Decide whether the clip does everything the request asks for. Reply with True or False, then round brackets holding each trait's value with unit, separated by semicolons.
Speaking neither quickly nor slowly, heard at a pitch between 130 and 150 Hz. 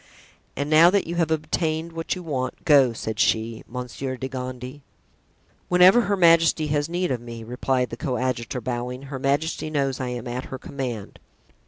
True (175 wpm; 135 Hz)